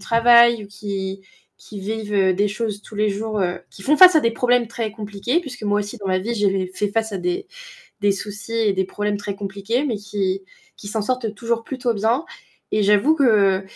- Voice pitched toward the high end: Yes, high, 210 Hz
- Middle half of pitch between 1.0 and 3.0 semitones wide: Yes, average, 2.7 semitones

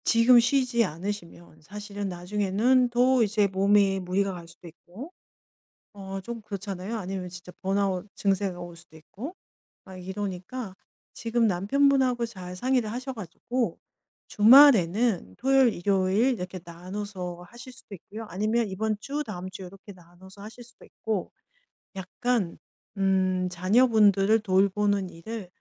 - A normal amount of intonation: Yes, average, 3.9 semitones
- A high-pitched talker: Yes, high, 200 Hz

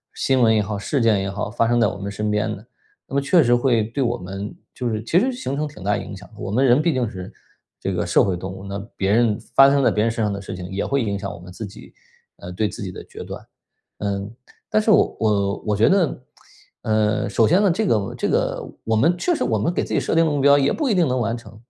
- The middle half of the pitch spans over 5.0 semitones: Yes, wide, 5.5 semitones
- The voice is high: No, low, 110 Hz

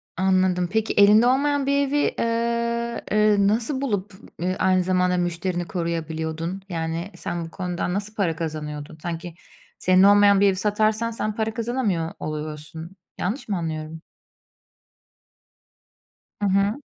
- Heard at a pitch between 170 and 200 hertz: Yes, high, 190 Hz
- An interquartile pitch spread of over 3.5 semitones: Yes, average, 4.5 semitones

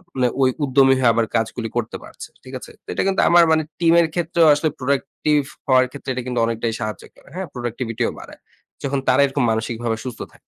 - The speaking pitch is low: Yes, low, 130 Hz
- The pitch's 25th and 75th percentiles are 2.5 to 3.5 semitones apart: No, average, 4.0 semitones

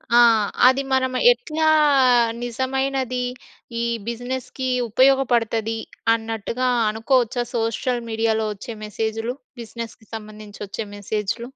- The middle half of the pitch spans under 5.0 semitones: Yes, narrow, 2.6 semitones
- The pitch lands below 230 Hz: No, high, 235 Hz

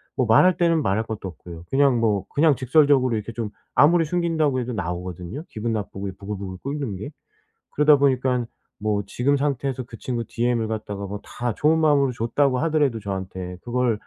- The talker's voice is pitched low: Yes, low, 120 Hz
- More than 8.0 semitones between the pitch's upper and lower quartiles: No, wide, 5.5 semitones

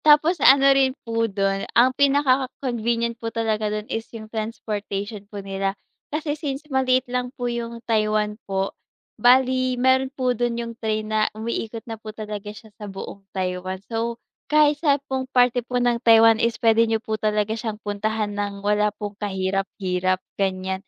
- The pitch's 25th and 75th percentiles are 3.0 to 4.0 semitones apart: Yes, average, 3.3 semitones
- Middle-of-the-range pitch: No, high, 225 Hz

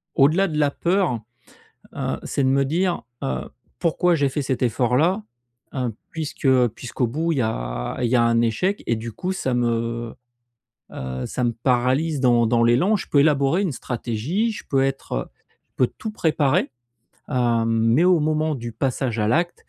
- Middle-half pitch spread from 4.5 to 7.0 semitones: Yes, average, 5.1 semitones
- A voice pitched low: Yes, low, 130 Hz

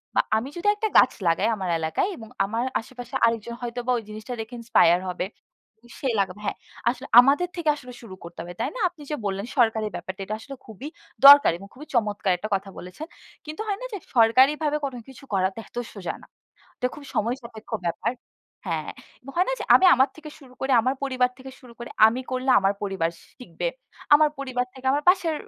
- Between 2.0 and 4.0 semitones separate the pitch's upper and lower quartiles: No, average, 5.2 semitones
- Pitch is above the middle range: Yes, high, 245 Hz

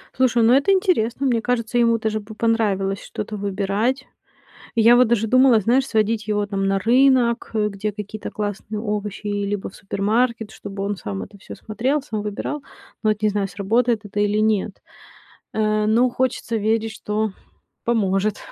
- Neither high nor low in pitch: No, high, 215 Hz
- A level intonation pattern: Yes, narrow, 2.3 semitones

